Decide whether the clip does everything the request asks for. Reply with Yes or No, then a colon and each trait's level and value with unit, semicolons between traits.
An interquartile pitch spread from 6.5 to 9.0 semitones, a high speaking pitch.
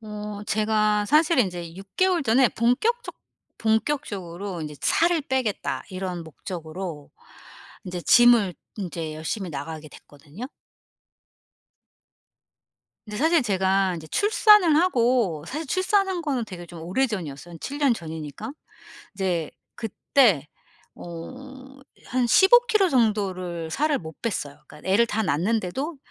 Yes: wide, 7.6 semitones; high, 210 Hz